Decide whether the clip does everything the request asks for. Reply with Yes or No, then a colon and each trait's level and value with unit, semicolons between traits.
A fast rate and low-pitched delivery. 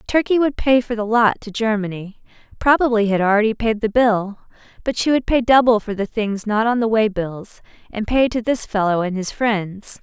No: fast, 210 wpm; high, 220 Hz